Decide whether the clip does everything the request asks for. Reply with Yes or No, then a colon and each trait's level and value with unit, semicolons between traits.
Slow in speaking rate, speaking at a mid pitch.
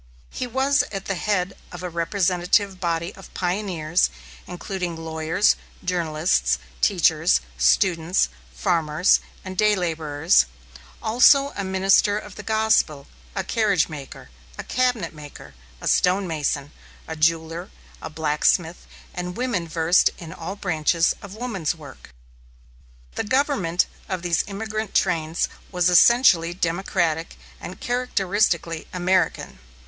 Yes: slow, 120 wpm; medium, 180 Hz